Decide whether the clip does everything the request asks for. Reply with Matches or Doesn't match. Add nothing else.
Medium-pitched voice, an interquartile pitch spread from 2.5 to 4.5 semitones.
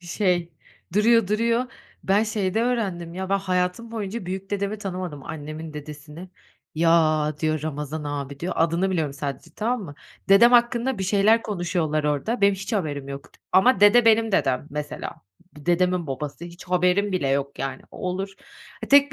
Doesn't match